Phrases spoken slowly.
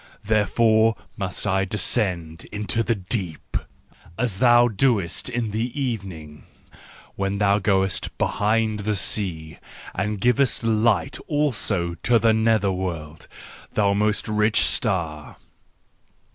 Yes: slow, 115 wpm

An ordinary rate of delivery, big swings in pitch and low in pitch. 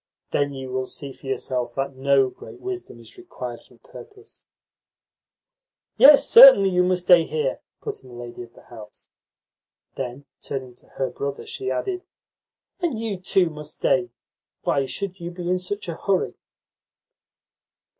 No: average, 160 wpm; wide, 7.8 semitones; medium, 170 Hz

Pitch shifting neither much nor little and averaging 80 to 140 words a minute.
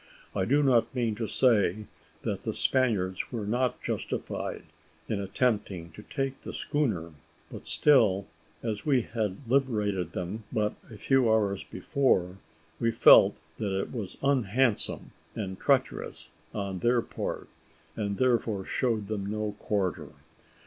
Yes: average, 4.1 semitones; slow, 135 wpm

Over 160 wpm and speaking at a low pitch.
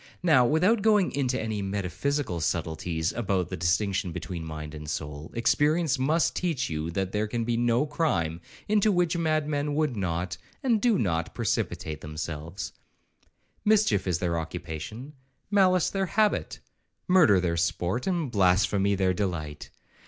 No: average, 145 wpm; low, 105 Hz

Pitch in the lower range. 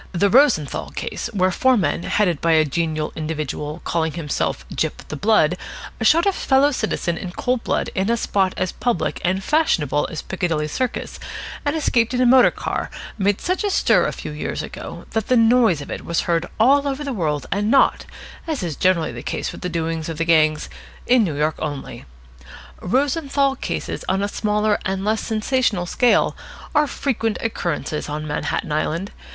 No: high, 190 Hz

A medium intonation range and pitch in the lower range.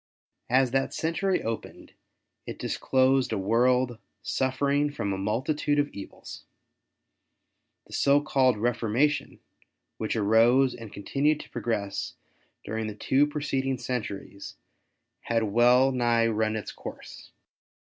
Yes: average, 3.4 semitones; low, 125 Hz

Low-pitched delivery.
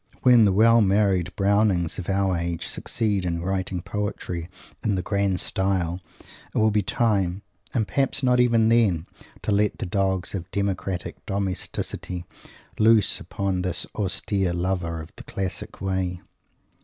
Yes: very low, 95 Hz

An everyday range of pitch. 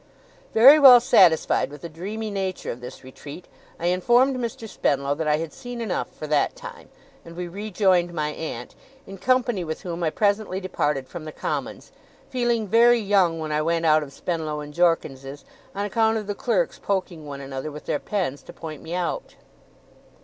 No: wide, 5.9 semitones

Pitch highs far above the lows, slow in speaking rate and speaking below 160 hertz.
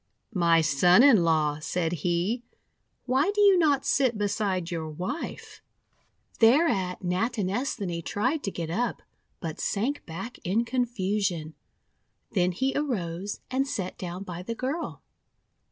No: wide, 6.4 semitones; slow, 130 wpm; high, 195 Hz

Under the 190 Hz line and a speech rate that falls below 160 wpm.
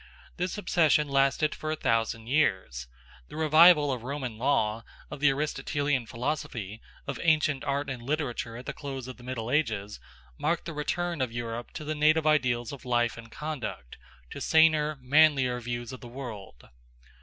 No: low, 135 Hz; average, 165 wpm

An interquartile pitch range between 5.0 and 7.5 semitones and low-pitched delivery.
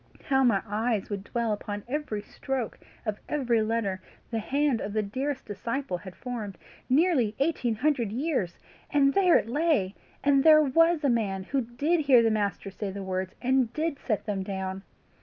No: average, 5.3 semitones; high, 235 Hz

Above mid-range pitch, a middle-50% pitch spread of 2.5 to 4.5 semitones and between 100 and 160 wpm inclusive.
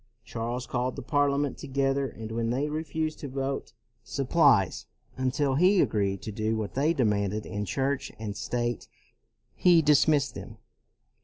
No: low, 130 Hz; average, 4.2 semitones; average, 150 wpm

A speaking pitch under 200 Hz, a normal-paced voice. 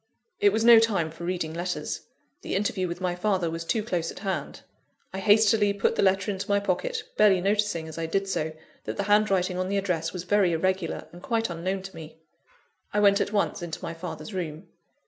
No: high, 190 Hz; fast, 210 wpm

